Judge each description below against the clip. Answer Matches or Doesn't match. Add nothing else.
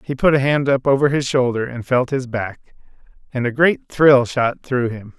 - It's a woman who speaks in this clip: Doesn't match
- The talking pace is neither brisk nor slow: Doesn't match